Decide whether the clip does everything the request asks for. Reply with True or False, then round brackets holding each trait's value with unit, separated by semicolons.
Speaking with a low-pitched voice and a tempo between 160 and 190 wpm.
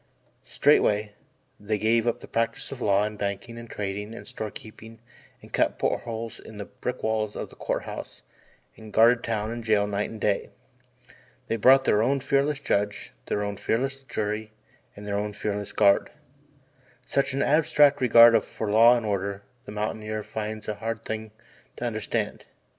True (110 Hz; 175 wpm)